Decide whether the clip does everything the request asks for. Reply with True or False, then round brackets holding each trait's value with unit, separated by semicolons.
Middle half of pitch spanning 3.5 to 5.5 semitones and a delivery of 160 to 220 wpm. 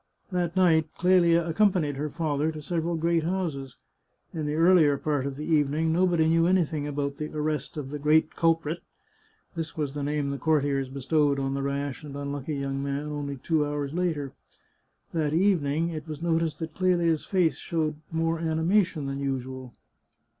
False (2.8 semitones; 175 wpm)